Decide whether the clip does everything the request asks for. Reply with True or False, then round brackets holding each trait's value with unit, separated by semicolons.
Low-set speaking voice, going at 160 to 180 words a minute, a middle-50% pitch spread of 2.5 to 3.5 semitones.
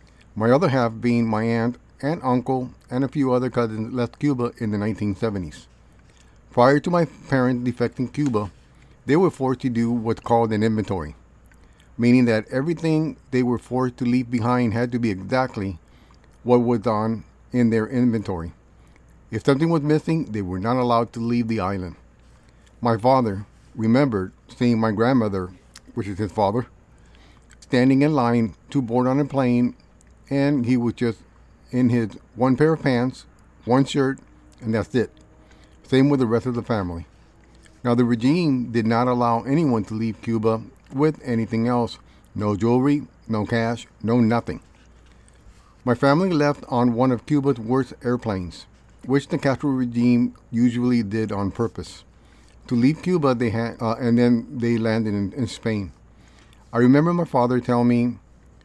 True (120 Hz; 165 wpm; 2.8 semitones)